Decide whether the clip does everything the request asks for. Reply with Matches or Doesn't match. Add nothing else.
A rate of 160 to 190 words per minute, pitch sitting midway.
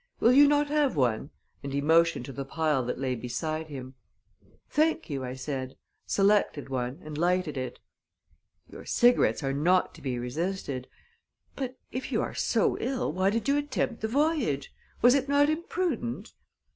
Matches